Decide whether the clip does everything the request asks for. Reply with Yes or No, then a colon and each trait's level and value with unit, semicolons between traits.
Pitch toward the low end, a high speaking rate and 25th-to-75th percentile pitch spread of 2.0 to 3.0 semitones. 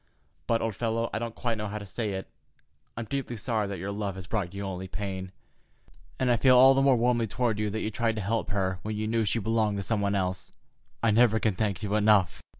Yes: low, 110 Hz; fast, 240 wpm; narrow, 2.6 semitones